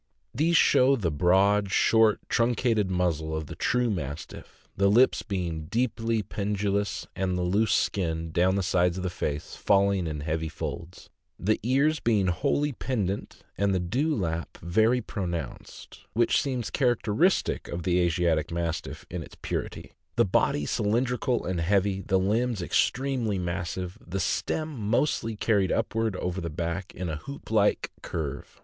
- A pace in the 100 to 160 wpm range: Yes, average, 150 wpm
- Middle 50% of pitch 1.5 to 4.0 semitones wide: No, average, 4.7 semitones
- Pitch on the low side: Yes, low, 100 Hz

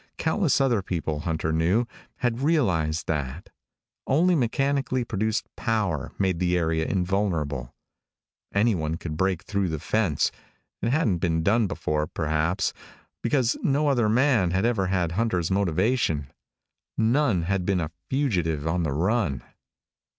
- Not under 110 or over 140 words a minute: Yes, slow, 135 wpm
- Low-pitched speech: Yes, very low, 95 Hz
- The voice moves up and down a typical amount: No, wide, 6.2 semitones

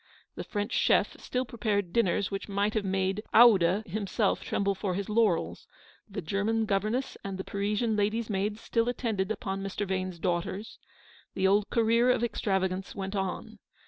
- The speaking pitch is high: Yes, high, 200 Hz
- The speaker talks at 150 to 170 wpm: Yes, average, 160 wpm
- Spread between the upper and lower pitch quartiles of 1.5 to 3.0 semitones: Yes, narrow, 2.4 semitones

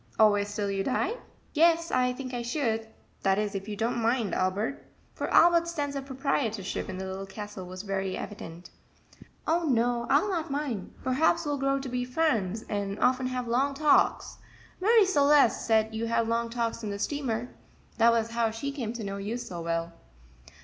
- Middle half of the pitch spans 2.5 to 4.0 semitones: No, average, 5.1 semitones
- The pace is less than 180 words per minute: No, average, 185 wpm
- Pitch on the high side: Yes, high, 235 Hz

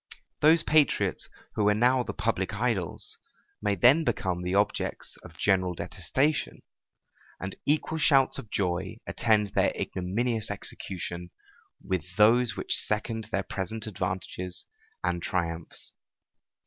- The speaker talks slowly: Yes, slow, 120 wpm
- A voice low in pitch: Yes, low, 105 Hz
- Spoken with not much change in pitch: No, average, 4.6 semitones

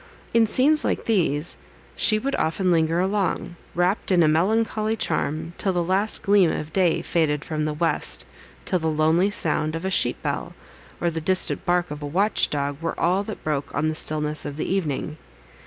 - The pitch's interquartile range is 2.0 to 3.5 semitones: No, average, 3.9 semitones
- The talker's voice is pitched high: No, medium, 170 Hz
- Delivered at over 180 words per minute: Yes, average, 190 wpm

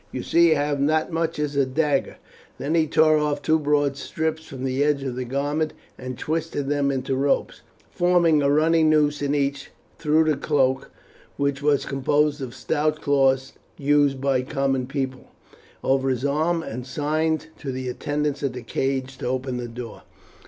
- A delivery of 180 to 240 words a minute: Yes, average, 190 wpm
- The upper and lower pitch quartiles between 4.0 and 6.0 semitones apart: No, narrow, 2.4 semitones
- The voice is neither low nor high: Yes, medium, 145 Hz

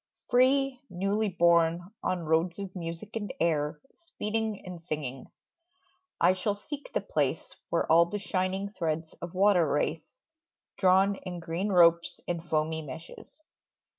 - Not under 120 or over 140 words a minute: Yes, slow, 135 wpm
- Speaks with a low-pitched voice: No, medium, 180 Hz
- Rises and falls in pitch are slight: No, average, 3.5 semitones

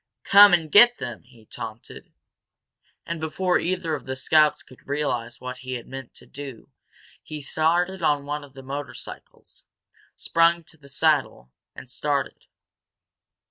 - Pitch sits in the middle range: Yes, medium, 145 Hz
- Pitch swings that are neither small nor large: Yes, average, 4.2 semitones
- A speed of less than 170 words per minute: Yes, average, 140 wpm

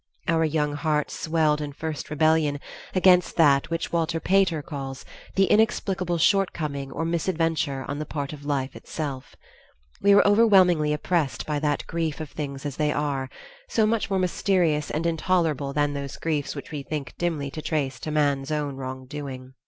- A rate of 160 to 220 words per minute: Yes, average, 170 wpm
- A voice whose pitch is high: No, medium, 150 Hz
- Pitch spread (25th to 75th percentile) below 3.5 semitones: Yes, average, 2.8 semitones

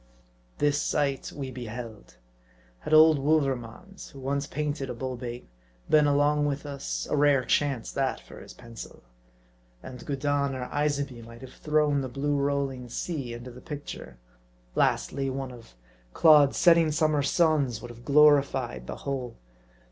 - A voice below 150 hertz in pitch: Yes, medium, 140 Hz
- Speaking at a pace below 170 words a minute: Yes, average, 150 wpm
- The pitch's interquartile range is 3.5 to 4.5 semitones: No, average, 2.8 semitones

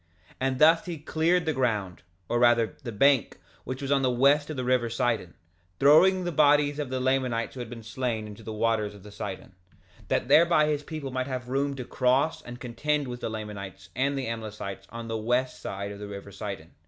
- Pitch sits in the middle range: No, low, 125 Hz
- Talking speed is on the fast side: Yes, fast, 215 wpm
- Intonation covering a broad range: No, average, 4.3 semitones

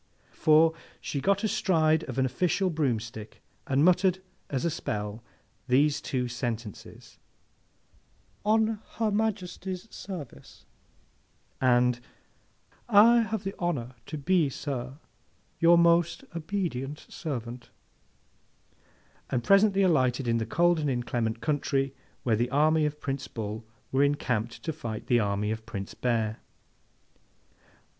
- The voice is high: No, medium, 140 Hz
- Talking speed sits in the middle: No, slow, 120 wpm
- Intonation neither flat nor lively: No, wide, 6.3 semitones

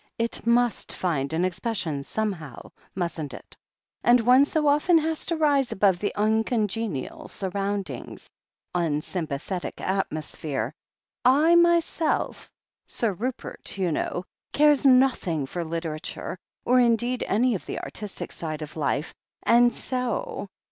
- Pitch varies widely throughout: Yes, wide, 6.9 semitones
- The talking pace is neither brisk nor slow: No, slow, 125 wpm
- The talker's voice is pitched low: No, high, 210 Hz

